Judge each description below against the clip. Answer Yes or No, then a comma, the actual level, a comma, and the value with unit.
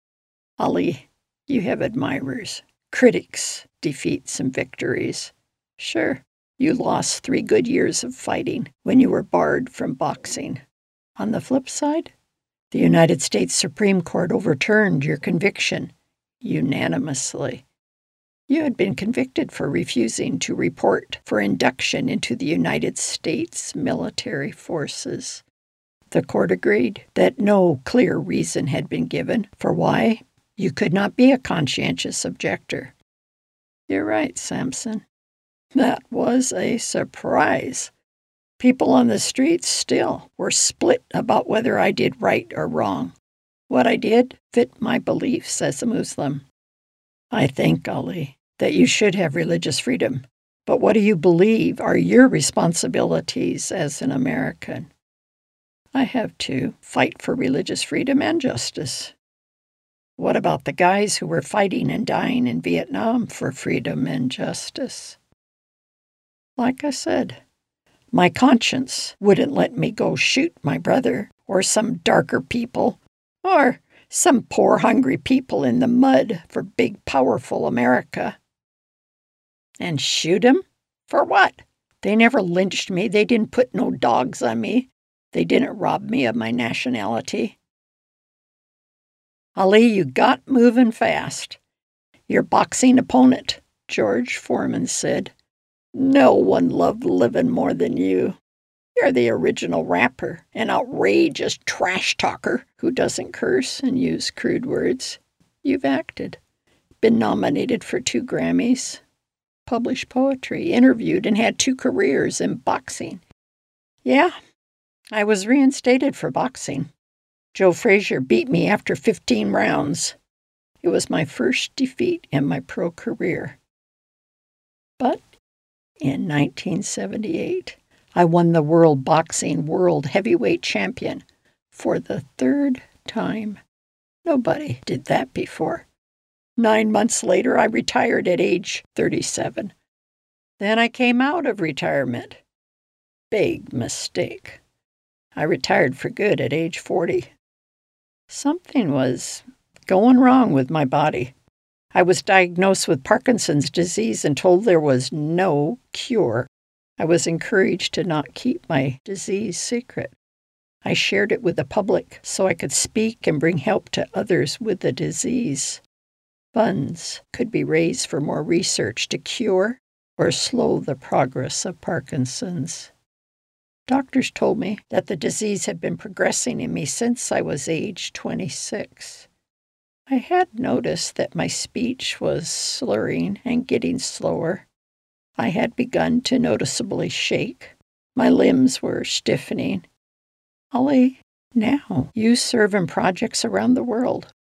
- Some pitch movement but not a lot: No, wide, 6.3 semitones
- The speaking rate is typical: No, slow, 130 wpm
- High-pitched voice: Yes, high, 225 Hz